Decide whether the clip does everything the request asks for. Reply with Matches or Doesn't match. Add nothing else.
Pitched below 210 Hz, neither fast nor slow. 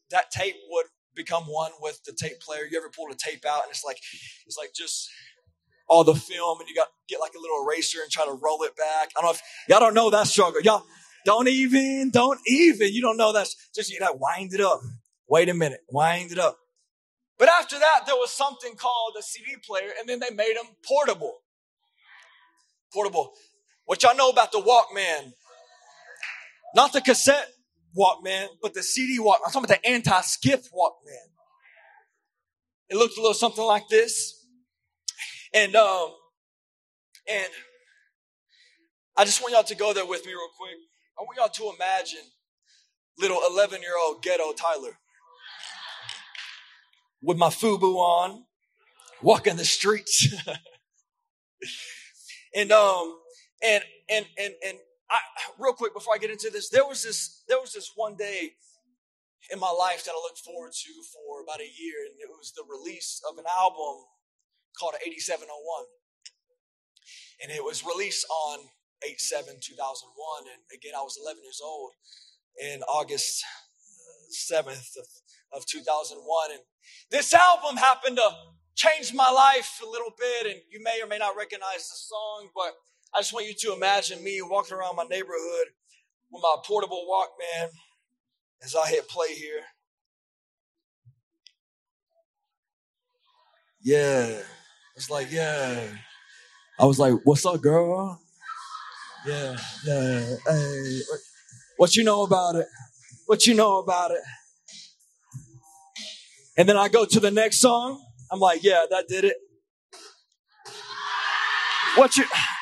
Doesn't match